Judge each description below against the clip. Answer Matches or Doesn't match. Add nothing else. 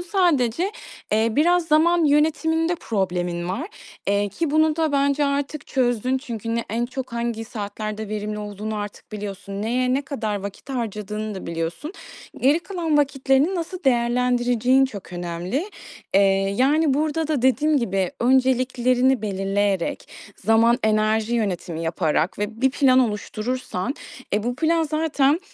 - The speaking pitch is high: Matches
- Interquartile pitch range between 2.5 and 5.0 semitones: Doesn't match